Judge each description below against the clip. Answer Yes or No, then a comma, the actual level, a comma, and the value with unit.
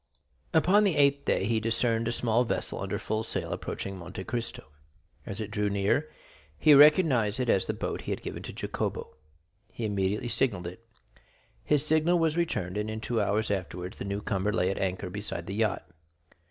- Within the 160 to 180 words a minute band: No, average, 190 wpm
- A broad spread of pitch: No, average, 4.5 semitones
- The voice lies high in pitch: No, low, 110 Hz